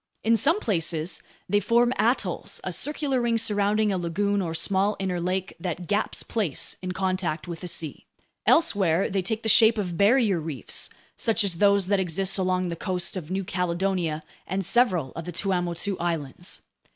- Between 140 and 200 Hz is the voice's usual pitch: Yes, high, 190 Hz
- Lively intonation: No, average, 3.2 semitones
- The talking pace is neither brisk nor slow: Yes, average, 175 wpm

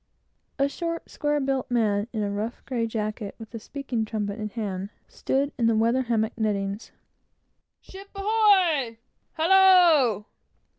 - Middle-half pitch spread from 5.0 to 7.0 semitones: Yes, wide, 5.6 semitones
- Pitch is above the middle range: Yes, high, 235 Hz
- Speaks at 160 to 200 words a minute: No, average, 140 wpm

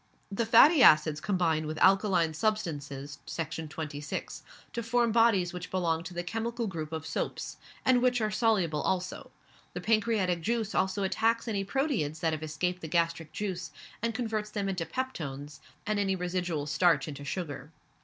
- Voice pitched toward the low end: No, medium, 180 Hz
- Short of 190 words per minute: Yes, average, 165 wpm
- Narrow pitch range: No, wide, 5.6 semitones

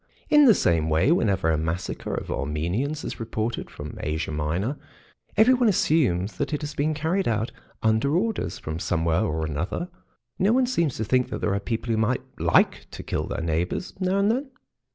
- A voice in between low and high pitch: No, low, 110 Hz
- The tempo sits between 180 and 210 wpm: Yes, average, 190 wpm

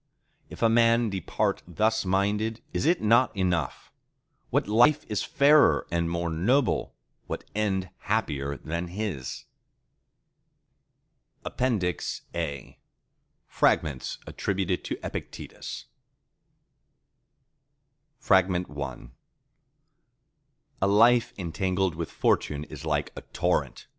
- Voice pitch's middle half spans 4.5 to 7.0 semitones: Yes, average, 4.8 semitones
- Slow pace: Yes, slow, 95 wpm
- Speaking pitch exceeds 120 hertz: No, very low, 95 Hz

